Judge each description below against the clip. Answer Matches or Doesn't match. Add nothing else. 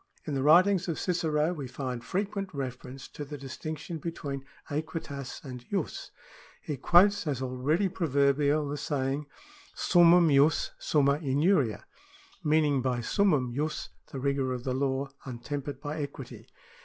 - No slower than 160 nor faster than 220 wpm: Doesn't match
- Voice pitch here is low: Doesn't match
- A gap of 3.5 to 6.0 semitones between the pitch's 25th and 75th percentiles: Doesn't match